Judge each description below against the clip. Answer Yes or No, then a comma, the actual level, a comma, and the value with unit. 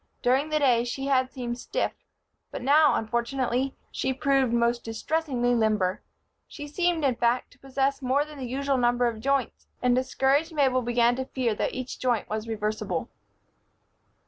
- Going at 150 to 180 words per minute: Yes, average, 165 wpm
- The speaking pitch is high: Yes, very high, 255 Hz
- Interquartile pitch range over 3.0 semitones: No, narrow, 2.6 semitones